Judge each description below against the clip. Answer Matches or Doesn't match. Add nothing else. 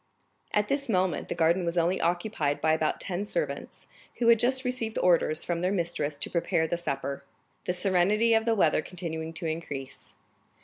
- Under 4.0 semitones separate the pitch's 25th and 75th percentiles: Doesn't match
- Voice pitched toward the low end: Doesn't match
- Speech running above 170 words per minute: Matches